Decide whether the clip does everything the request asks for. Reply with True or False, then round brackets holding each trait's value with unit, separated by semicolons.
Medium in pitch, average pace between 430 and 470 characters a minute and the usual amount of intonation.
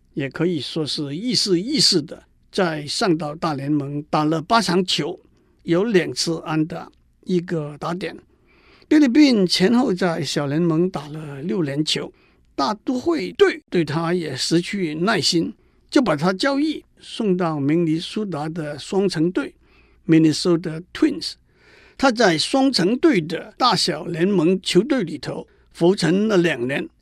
False (175 Hz; 225 characters per minute; 3.6 semitones)